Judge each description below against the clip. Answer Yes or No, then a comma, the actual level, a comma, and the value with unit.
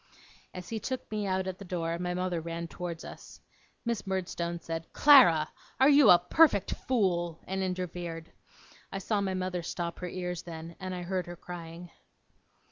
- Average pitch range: No, narrow, 2.0 semitones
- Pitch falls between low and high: Yes, medium, 180 Hz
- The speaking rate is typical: Yes, average, 175 wpm